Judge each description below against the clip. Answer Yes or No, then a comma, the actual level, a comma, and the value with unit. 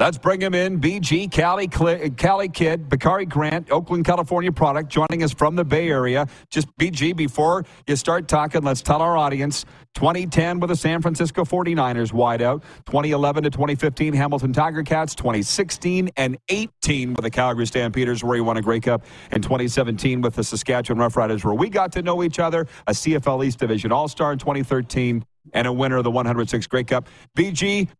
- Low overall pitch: No, medium, 150 Hz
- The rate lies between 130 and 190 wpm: Yes, average, 180 wpm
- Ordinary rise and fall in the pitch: Yes, average, 5.0 semitones